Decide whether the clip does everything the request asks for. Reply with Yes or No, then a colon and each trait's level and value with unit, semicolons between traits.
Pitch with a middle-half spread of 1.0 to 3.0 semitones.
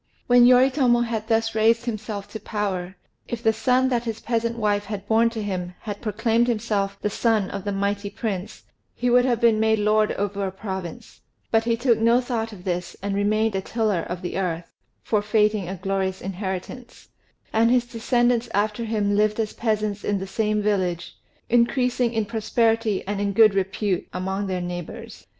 Yes: average, 2.7 semitones